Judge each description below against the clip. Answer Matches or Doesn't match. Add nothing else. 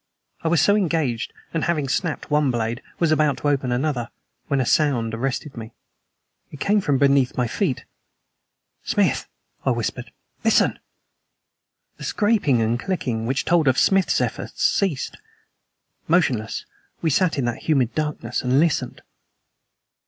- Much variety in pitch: Doesn't match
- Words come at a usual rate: Matches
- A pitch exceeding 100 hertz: Matches